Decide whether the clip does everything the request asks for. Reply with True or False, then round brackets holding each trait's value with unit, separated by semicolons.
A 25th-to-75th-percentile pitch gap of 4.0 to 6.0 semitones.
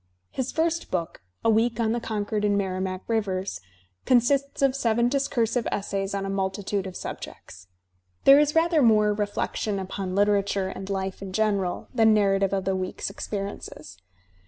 False (3.2 semitones)